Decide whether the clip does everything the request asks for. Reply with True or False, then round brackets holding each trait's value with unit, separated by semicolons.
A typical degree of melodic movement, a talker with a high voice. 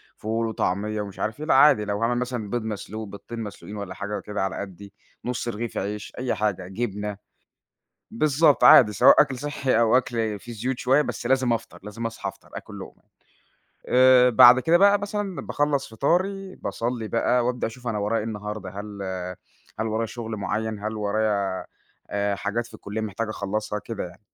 False (3.2 semitones; 110 Hz)